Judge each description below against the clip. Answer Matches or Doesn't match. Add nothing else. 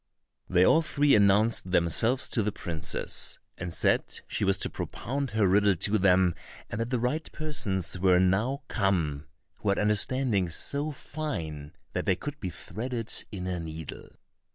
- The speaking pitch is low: Matches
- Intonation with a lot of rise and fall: Matches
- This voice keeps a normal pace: Matches